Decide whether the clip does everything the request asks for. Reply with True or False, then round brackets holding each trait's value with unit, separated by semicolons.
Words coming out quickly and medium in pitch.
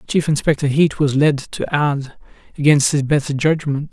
False (170 wpm; 145 Hz)